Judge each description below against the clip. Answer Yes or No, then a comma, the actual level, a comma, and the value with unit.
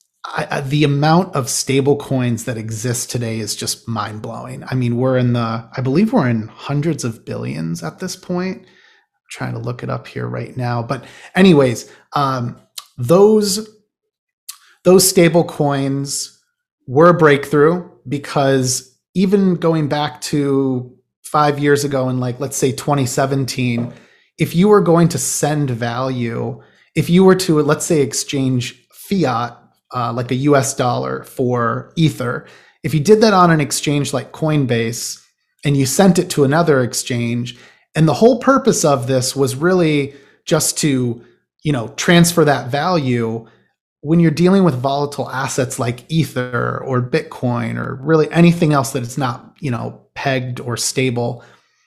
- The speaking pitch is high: No, medium, 140 Hz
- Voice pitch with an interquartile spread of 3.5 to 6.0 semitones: Yes, average, 4.4 semitones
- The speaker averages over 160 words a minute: No, average, 155 wpm